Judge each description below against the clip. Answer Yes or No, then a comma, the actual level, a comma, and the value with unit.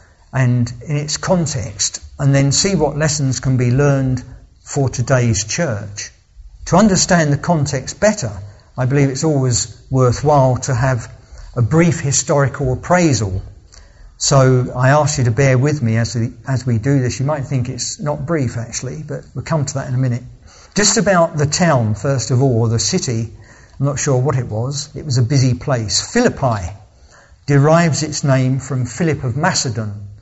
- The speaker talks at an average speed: Yes, average, 175 wpm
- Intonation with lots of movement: No, average, 3.7 semitones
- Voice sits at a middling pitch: No, low, 130 Hz